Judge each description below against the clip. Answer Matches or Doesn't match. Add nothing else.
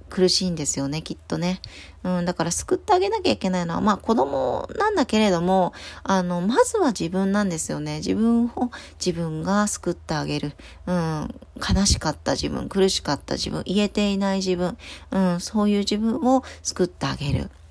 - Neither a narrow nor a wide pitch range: Matches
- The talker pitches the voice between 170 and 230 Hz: Matches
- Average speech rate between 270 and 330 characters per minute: Doesn't match